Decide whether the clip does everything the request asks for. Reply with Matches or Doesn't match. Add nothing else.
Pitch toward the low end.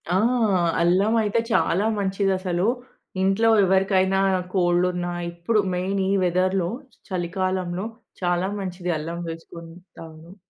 Doesn't match